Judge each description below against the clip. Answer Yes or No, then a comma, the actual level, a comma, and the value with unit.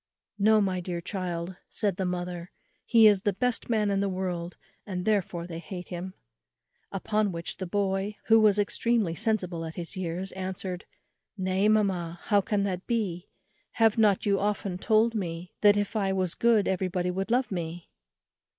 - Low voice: No, high, 190 Hz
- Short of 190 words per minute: Yes, average, 170 wpm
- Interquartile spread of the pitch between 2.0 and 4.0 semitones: Yes, average, 2.7 semitones